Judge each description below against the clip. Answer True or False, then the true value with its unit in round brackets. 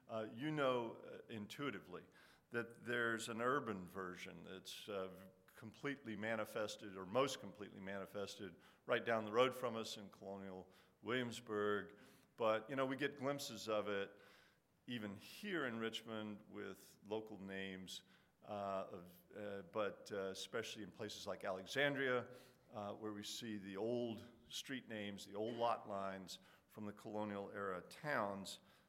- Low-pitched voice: True (105 Hz)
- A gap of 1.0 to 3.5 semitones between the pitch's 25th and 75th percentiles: True (3.0 semitones)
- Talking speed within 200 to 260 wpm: False (145 wpm)